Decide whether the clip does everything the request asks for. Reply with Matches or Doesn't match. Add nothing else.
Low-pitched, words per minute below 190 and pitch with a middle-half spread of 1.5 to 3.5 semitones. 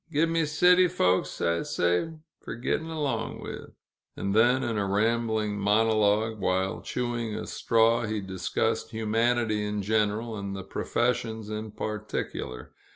Matches